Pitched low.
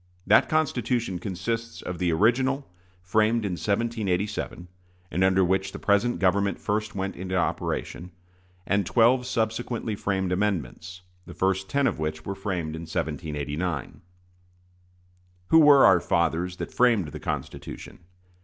Yes: very low, 95 Hz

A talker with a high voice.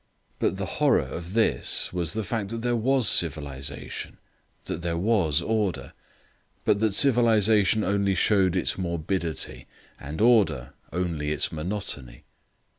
No: very low, 95 Hz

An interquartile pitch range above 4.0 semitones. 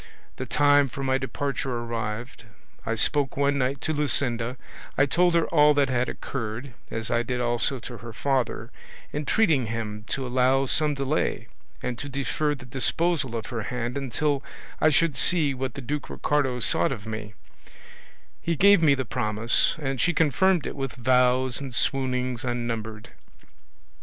No: average, 3.2 semitones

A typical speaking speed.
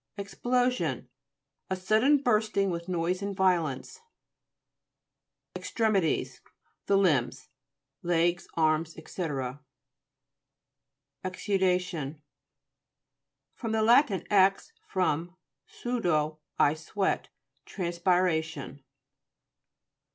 No: slow, 70 wpm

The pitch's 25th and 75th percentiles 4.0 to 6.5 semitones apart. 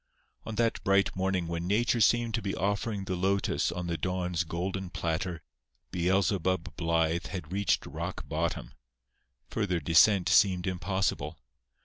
No: narrow, 2.6 semitones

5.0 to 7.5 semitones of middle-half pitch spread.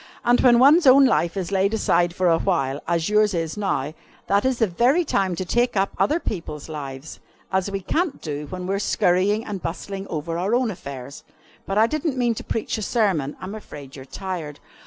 Yes: average, 5.3 semitones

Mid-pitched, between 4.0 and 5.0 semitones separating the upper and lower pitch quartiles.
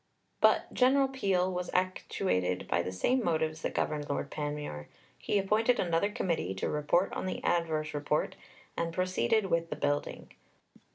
Yes: medium, 170 Hz; average, 4.3 semitones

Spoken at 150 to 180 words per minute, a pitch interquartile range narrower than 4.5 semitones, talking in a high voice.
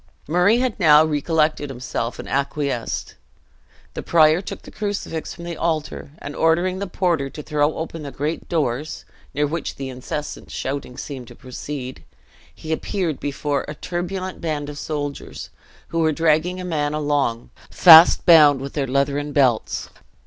No: average, 155 wpm; average, 2.9 semitones; medium, 150 Hz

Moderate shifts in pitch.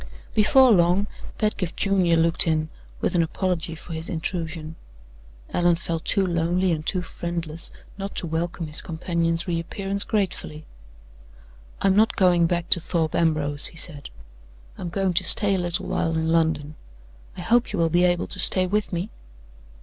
No: narrow, 2.3 semitones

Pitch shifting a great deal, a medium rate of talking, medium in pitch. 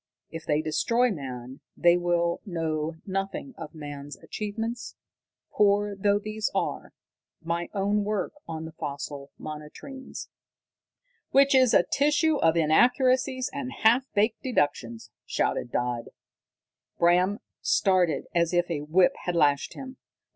No: wide, 6.7 semitones; slow, 130 wpm; medium, 180 Hz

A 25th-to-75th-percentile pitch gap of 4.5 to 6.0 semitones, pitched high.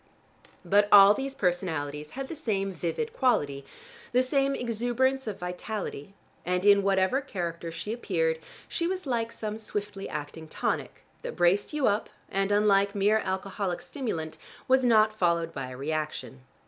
Yes: wide, 5.5 semitones; high, 200 Hz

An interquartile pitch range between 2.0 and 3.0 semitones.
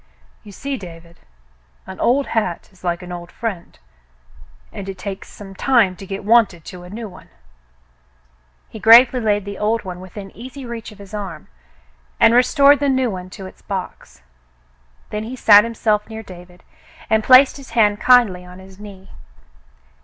No: average, 3.9 semitones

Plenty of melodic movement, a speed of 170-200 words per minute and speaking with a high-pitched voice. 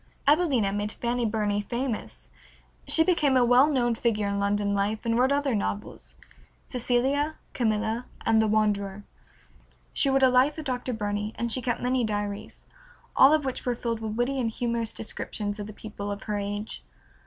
No: average, 3.6 semitones; average, 175 wpm; high, 230 Hz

